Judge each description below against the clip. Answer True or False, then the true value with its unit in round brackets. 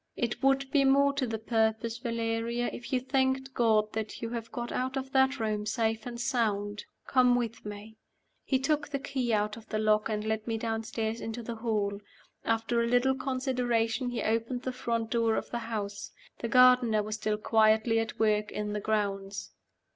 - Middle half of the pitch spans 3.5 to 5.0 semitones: False (2.5 semitones)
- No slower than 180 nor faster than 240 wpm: True (190 wpm)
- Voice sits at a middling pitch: False (230 Hz)